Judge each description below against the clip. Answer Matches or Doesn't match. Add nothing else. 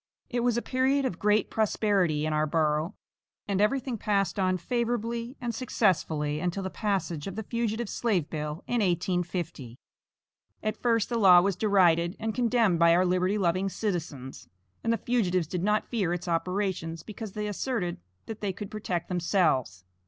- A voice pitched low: Doesn't match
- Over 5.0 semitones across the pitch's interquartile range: Doesn't match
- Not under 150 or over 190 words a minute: Matches